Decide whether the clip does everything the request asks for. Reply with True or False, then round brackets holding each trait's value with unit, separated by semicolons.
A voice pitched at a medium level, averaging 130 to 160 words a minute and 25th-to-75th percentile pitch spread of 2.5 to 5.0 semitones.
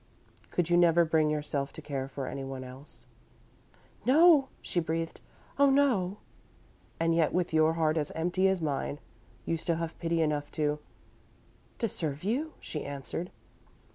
True (165 Hz; 155 wpm; 3.3 semitones)